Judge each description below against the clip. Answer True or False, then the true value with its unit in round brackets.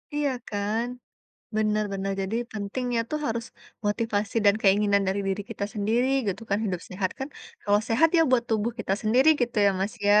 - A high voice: True (215 Hz)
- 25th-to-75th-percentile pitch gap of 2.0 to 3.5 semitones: True (2.7 semitones)